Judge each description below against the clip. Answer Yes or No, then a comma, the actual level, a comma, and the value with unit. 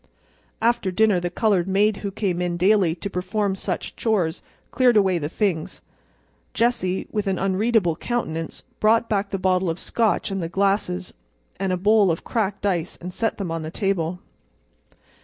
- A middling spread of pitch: Yes, average, 3.2 semitones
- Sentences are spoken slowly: No, average, 170 wpm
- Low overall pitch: No, high, 195 Hz